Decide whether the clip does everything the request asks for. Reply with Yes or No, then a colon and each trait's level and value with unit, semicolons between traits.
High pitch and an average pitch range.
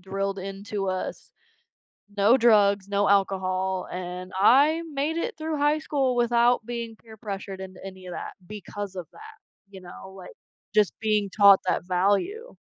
Yes: high, 200 Hz; average, 4.0 semitones